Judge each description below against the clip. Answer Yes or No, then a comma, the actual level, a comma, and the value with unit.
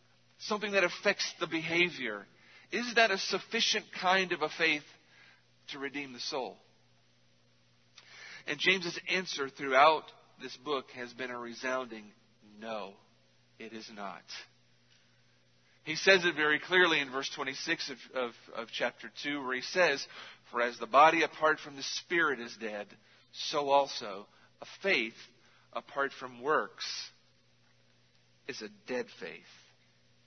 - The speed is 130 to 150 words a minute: Yes, slow, 135 wpm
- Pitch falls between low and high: No, low, 125 Hz